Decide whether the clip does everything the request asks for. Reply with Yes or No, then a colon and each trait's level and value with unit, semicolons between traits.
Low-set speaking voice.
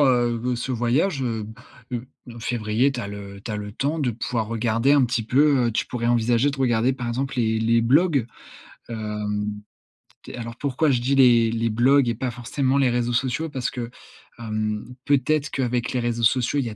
Yes: low, 120 Hz